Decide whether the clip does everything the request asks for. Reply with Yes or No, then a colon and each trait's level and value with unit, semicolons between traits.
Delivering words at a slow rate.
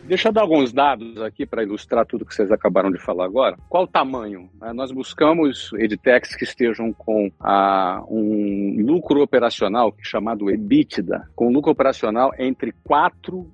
No: average, 160 wpm